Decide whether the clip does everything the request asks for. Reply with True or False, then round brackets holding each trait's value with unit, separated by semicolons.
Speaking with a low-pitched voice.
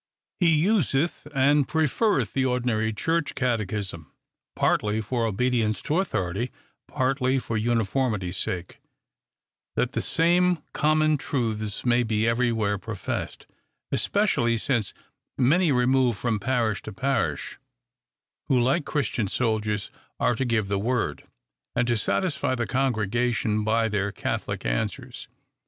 True (120 Hz)